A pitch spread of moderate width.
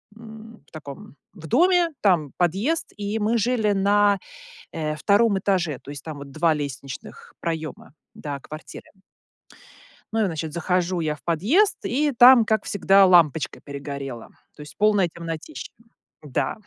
No: wide, 6.2 semitones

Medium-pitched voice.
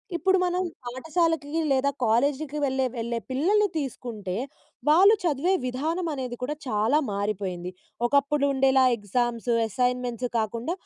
No: very high, 265 Hz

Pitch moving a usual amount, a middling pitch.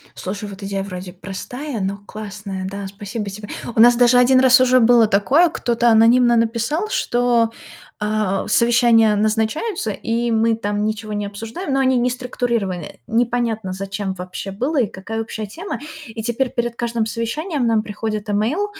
No: average, 3.1 semitones; high, 225 Hz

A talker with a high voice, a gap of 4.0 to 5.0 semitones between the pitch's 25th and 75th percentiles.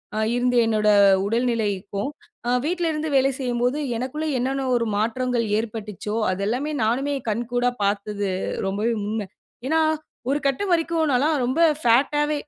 Yes: high, 245 Hz; average, 4.4 semitones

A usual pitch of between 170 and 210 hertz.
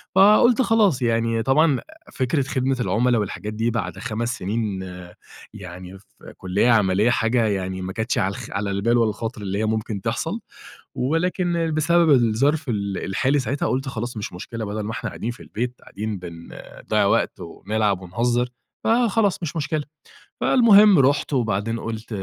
No: low, 115 Hz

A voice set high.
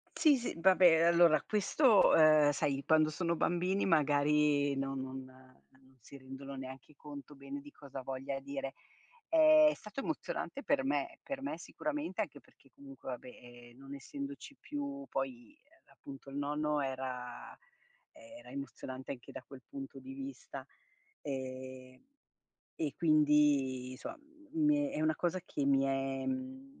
No: medium, 150 Hz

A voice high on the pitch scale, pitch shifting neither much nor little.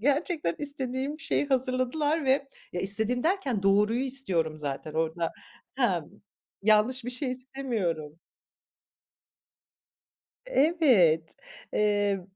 No: high, 245 Hz; wide, 6.2 semitones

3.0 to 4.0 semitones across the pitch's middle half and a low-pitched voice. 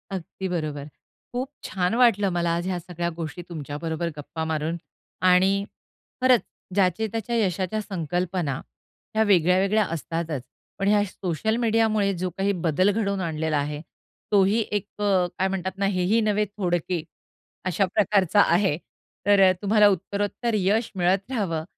No: average, 3.3 semitones; high, 190 Hz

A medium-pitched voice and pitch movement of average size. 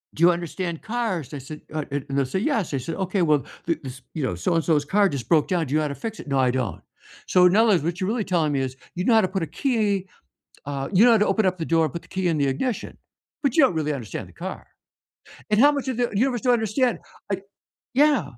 No: medium, 175 Hz; wide, 6.9 semitones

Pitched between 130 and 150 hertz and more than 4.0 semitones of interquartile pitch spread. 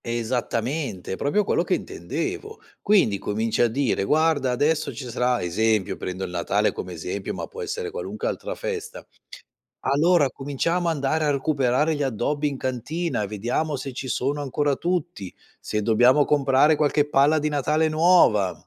Yes: medium, 140 Hz; average, 5.1 semitones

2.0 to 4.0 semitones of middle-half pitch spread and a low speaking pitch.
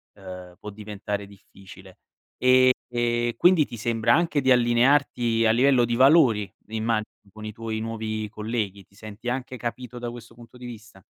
Yes: narrow, 2.5 semitones; low, 115 Hz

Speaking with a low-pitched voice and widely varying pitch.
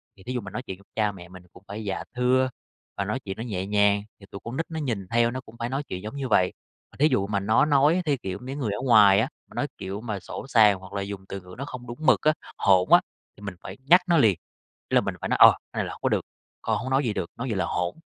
No: low, 110 Hz; average, 4.9 semitones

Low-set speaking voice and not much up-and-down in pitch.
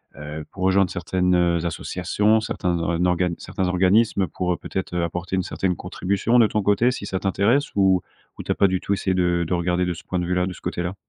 Yes: very low, 90 Hz; narrow, 1.8 semitones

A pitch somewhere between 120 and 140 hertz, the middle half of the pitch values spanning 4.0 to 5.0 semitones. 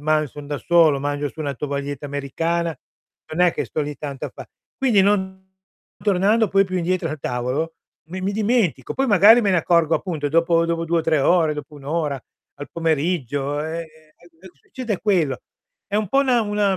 No: medium, 165 Hz; average, 4.6 semitones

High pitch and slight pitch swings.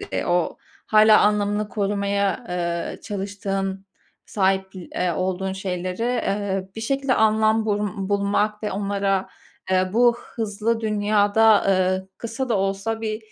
Yes: high, 205 Hz; narrow, 2.2 semitones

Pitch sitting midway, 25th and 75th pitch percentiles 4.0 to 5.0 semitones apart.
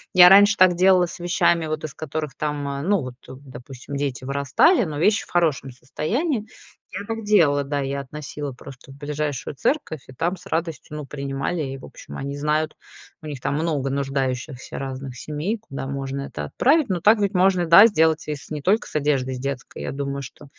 Yes: medium, 150 Hz; average, 4.5 semitones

